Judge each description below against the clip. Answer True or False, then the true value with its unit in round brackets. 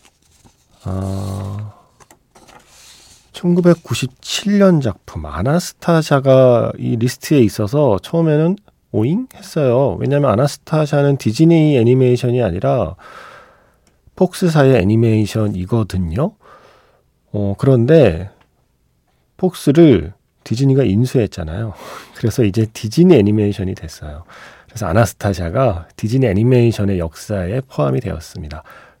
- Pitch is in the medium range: False (120 Hz)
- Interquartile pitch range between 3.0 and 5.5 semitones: False (6.1 semitones)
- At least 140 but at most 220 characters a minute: False (260 characters per minute)